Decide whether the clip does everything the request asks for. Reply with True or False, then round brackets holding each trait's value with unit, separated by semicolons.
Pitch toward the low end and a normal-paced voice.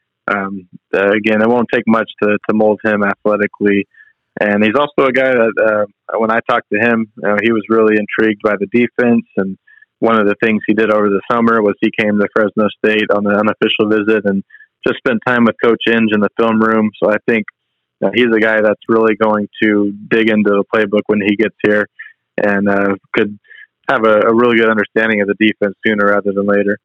False (105 Hz; 220 wpm)